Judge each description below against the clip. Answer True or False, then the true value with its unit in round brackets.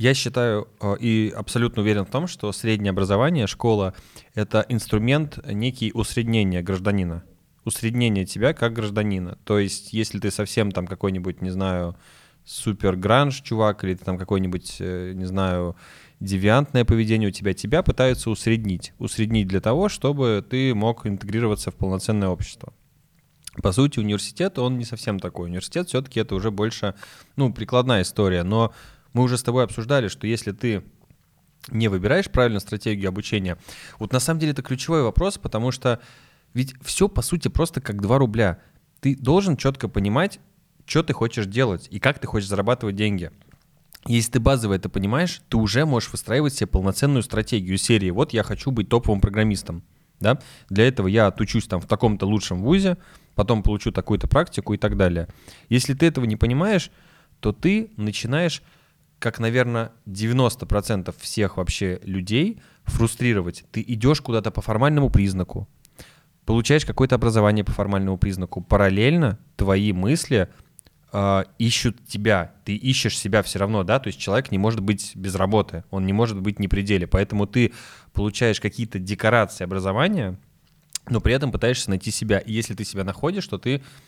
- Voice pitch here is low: True (110 Hz)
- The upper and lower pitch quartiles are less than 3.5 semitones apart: False (4.5 semitones)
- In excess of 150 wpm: True (160 wpm)